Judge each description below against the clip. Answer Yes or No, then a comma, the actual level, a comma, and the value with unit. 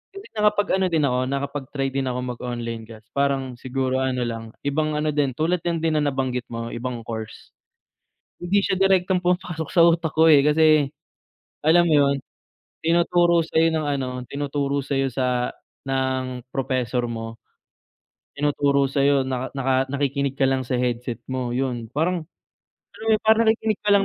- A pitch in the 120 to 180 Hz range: Yes, medium, 140 Hz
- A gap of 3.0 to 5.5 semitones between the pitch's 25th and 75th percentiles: Yes, average, 4.0 semitones